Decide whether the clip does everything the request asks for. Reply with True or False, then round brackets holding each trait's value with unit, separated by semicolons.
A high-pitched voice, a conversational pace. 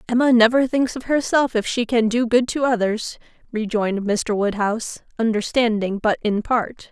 True (230 Hz; 165 wpm)